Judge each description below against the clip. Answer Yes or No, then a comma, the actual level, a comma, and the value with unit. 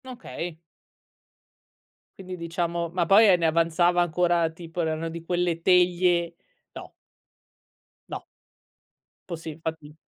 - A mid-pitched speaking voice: Yes, medium, 170 Hz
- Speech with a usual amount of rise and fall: No, narrow, 1.4 semitones